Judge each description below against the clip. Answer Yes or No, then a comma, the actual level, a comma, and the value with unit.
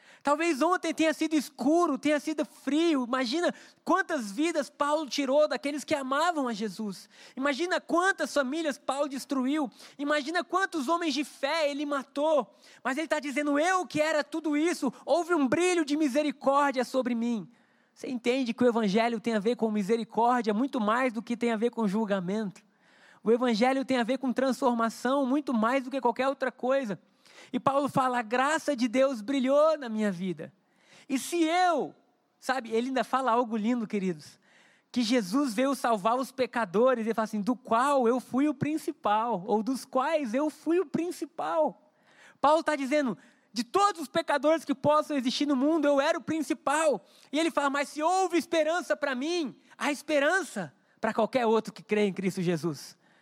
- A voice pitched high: Yes, very high, 270 Hz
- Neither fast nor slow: Yes, average, 175 wpm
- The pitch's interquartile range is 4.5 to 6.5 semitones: No, average, 4.1 semitones